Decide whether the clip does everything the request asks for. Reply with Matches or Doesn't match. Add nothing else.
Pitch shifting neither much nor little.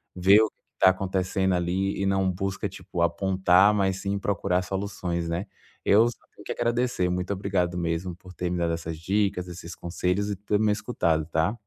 Doesn't match